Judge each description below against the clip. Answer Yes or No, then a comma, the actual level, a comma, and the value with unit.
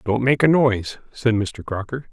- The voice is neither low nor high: No, low, 120 Hz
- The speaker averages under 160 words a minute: No, average, 200 wpm